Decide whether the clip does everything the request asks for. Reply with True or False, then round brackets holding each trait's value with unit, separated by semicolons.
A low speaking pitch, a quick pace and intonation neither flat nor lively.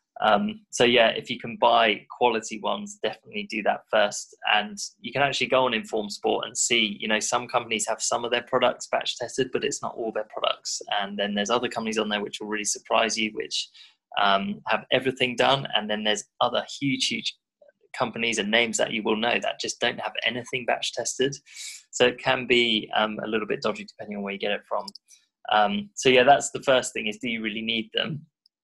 True (115 Hz; 220 wpm; 3.5 semitones)